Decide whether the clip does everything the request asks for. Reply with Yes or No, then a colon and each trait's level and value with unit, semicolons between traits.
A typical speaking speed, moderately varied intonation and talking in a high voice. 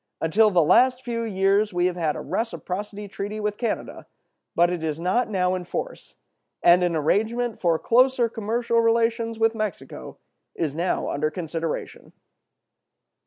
Yes: average, 150 wpm; average, 4.7 semitones; high, 205 Hz